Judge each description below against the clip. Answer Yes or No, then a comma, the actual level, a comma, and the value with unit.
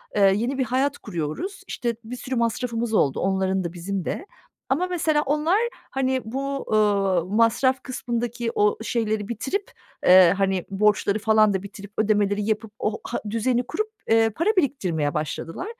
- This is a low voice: No, high, 220 Hz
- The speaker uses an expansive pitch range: No, average, 4.8 semitones